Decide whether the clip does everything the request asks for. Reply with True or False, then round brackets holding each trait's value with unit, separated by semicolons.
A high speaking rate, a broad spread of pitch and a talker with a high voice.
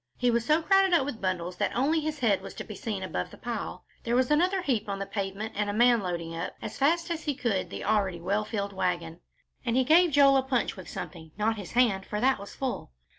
True (250 wpm; 5.9 semitones; 225 Hz)